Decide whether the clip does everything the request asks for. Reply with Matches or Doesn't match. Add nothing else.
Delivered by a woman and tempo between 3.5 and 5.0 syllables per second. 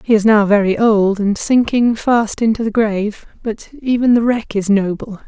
Matches